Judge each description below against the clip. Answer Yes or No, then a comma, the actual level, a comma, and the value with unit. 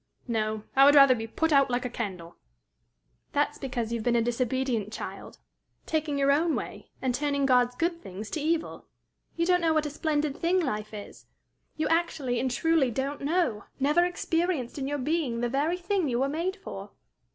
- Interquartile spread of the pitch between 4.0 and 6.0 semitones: Yes, average, 5.0 semitones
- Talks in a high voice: Yes, very high, 275 Hz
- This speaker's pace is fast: No, average, 195 wpm